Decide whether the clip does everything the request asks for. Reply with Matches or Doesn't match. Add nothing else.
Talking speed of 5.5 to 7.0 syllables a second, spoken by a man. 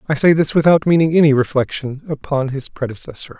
Matches